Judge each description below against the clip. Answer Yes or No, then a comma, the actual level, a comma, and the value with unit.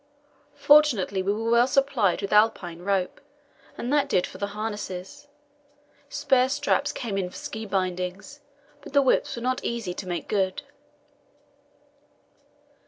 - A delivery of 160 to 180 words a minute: No, average, 145 wpm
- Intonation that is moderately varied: No, wide, 6.0 semitones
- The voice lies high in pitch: Yes, high, 215 Hz